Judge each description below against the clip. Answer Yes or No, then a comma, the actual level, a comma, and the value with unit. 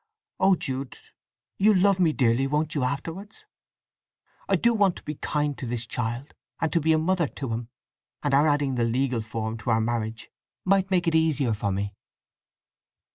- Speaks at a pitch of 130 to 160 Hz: Yes, medium, 140 Hz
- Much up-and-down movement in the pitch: Yes, wide, 5.8 semitones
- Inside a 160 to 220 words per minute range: Yes, average, 185 wpm